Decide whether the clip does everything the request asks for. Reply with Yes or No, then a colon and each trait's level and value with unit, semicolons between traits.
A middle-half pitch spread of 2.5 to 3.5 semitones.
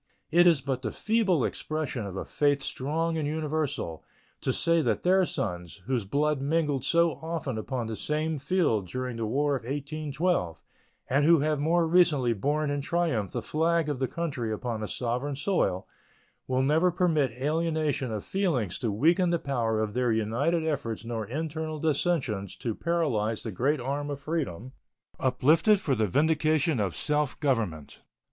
No: average, 5.3 semitones